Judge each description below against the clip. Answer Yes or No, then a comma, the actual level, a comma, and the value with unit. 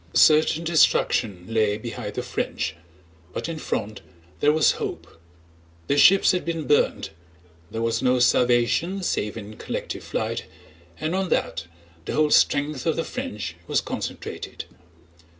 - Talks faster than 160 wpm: No, average, 140 wpm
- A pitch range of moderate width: No, wide, 6.7 semitones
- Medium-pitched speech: No, low, 130 Hz